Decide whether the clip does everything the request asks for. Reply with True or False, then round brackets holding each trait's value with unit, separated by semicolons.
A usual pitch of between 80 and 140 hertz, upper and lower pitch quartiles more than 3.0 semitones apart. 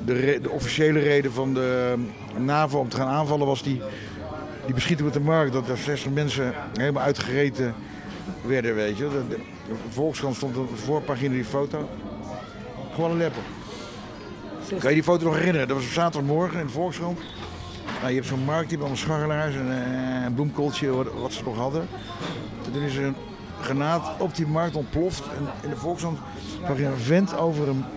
True (135 Hz; 3.7 semitones)